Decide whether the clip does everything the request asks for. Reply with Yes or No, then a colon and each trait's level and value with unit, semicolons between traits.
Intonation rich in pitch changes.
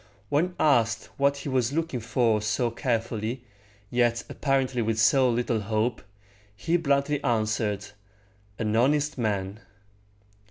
No: average, 3.9 semitones